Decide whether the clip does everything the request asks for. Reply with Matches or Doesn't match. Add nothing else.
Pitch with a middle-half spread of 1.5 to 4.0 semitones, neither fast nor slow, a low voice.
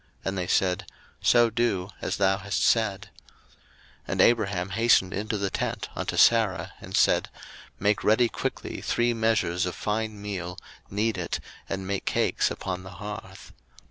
Matches